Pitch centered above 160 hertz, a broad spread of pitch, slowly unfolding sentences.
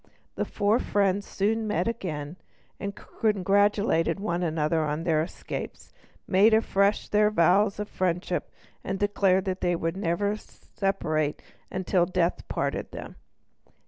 No: high, 190 Hz; average, 3.2 semitones; slow, 130 wpm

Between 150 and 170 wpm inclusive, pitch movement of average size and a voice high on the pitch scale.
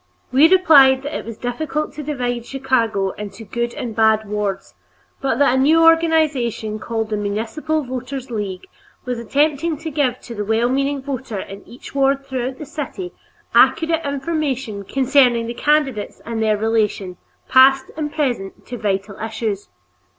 Yes: average, 160 wpm; average, 4.5 semitones; very high, 255 Hz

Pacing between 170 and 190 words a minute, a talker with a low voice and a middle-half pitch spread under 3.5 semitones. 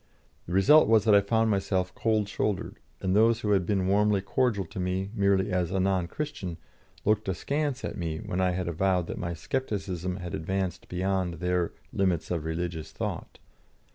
Yes: average, 180 wpm; very low, 95 Hz; narrow, 2.6 semitones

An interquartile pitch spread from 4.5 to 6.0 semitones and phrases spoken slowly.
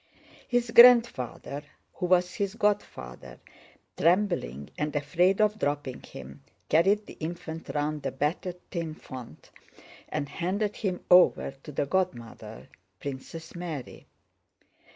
Yes: average, 5.2 semitones; slow, 115 wpm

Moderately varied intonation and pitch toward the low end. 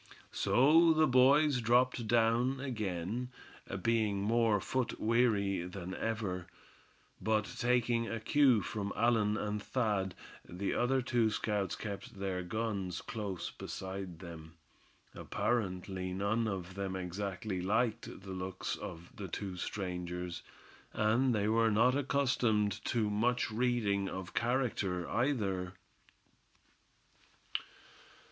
Yes: average, 4.1 semitones; low, 105 Hz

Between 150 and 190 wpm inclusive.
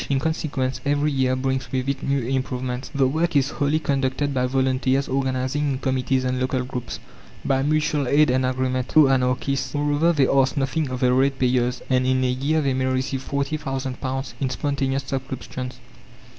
Yes: average, 170 wpm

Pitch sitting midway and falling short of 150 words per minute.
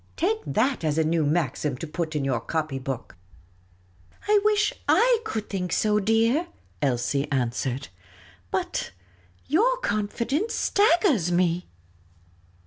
Yes: medium, 170 Hz; slow, 135 wpm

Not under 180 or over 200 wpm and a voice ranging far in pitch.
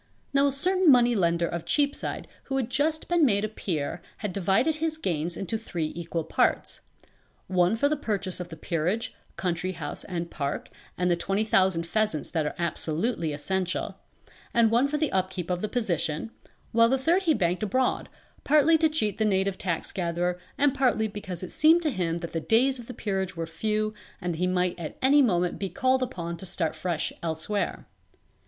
Yes: average, 195 wpm; wide, 6.6 semitones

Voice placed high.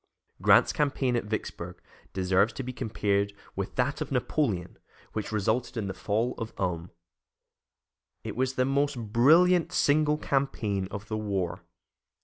No: low, 115 Hz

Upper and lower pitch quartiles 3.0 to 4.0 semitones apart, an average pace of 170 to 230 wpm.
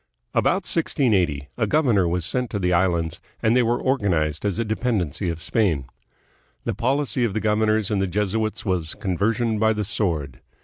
No: average, 4.4 semitones; average, 180 wpm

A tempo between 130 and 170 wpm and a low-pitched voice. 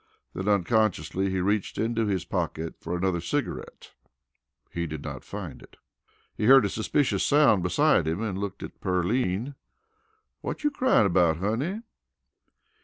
Yes: average, 145 wpm; low, 100 Hz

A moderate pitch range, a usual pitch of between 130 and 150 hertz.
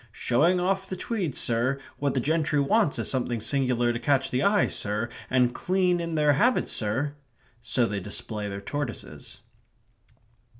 No: wide, 6.1 semitones; low, 135 Hz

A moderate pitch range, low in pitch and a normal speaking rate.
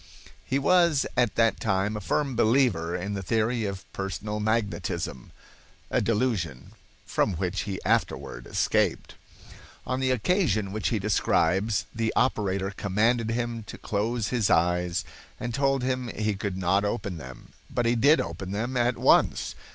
Yes: average, 3.9 semitones; low, 105 Hz; average, 150 wpm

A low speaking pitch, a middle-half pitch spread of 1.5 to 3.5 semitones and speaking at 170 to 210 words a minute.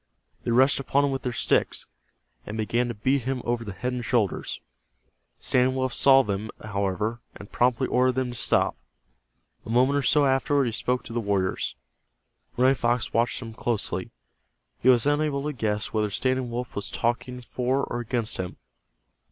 Yes: low, 120 Hz; average, 2.7 semitones; average, 175 wpm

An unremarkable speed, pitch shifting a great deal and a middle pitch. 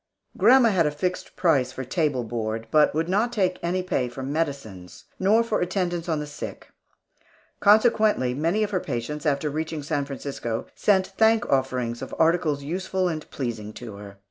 Yes: average, 170 wpm; wide, 6.2 semitones; medium, 155 Hz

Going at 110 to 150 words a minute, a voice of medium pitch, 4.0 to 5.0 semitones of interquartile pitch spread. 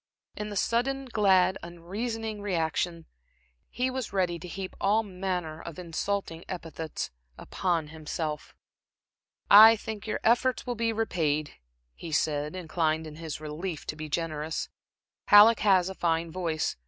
Yes: average, 140 wpm; medium, 180 Hz; average, 4.7 semitones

